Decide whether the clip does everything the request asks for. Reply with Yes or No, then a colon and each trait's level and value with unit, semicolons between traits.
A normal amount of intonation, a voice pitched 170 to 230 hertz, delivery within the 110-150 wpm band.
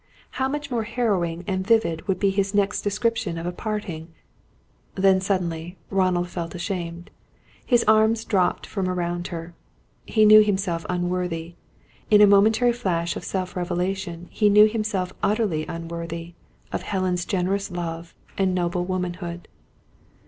Yes: average, 3.1 semitones; medium, 185 Hz; average, 140 wpm